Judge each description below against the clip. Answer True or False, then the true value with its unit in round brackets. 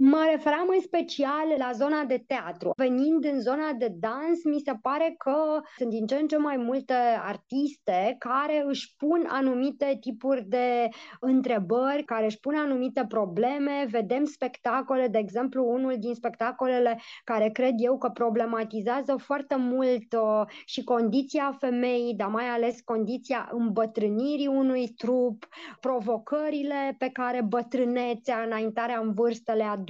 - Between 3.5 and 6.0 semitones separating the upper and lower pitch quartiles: False (3.0 semitones)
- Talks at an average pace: True (140 wpm)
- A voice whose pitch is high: True (255 Hz)